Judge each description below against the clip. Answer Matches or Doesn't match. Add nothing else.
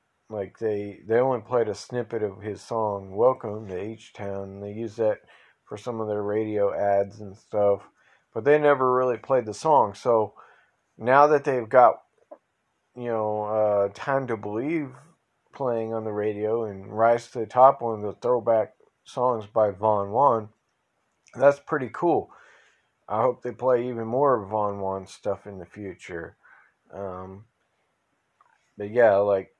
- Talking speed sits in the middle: Matches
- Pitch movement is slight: Doesn't match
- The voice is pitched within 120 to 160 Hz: Doesn't match